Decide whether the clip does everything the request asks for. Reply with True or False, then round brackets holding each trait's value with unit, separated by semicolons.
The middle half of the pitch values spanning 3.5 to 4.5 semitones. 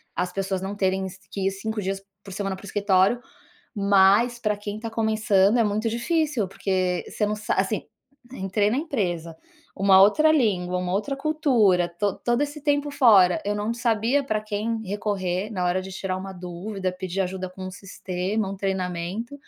False (3.0 semitones)